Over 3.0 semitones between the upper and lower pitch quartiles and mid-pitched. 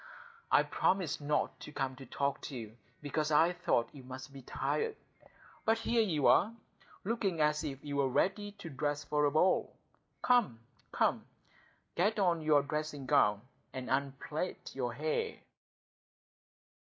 Yes: wide, 5.4 semitones; medium, 150 Hz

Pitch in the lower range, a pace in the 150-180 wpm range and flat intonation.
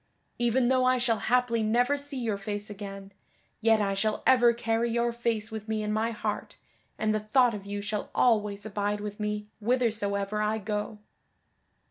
No: high, 215 Hz; average, 175 wpm; narrow, 2.3 semitones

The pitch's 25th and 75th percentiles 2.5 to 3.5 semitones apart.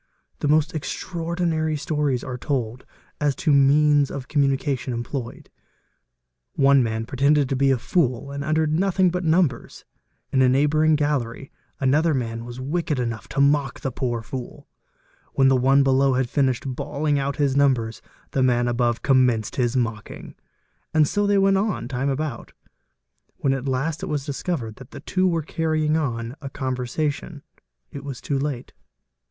Yes: average, 3.1 semitones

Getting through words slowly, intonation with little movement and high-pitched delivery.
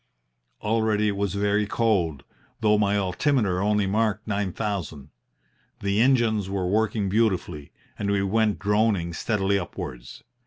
No: slow, 130 wpm; narrow, 2.2 semitones; low, 100 Hz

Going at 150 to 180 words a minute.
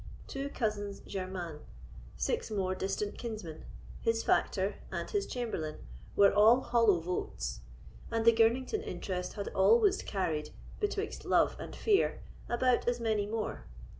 No: slow, 135 wpm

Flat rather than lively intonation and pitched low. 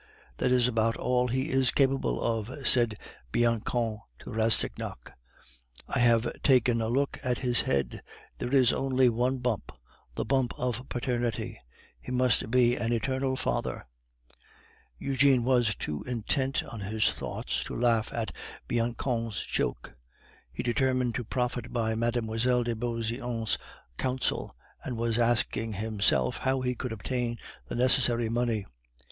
Yes: narrow, 2.0 semitones; low, 120 Hz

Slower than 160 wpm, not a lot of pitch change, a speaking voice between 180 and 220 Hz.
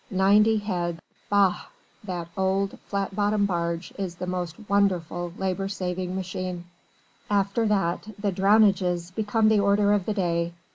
Yes: average, 140 wpm; narrow, 2.3 semitones; high, 190 Hz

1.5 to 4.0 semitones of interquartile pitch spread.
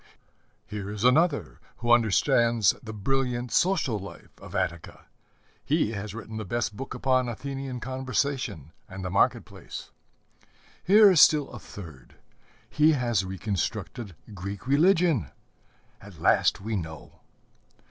No: average, 5.3 semitones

